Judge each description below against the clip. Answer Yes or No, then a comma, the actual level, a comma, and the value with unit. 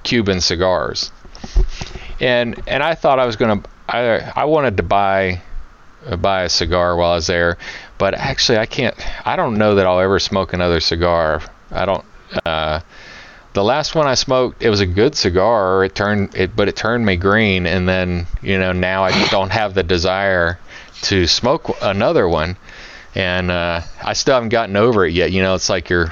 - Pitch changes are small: Yes, narrow, 2.2 semitones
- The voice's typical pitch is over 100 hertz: No, very low, 95 Hz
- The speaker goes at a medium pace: Yes, average, 190 wpm